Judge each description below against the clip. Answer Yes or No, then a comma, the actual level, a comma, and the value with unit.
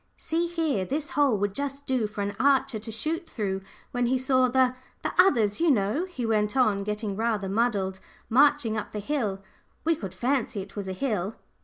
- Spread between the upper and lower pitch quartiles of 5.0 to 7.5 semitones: Yes, wide, 5.5 semitones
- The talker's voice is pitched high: Yes, high, 235 Hz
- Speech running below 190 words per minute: No, average, 195 wpm